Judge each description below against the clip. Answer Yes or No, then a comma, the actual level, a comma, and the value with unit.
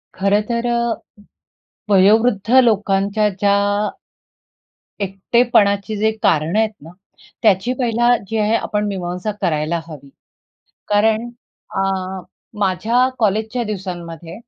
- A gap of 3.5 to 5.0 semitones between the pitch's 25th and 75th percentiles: No, average, 3.0 semitones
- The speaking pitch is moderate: No, high, 205 Hz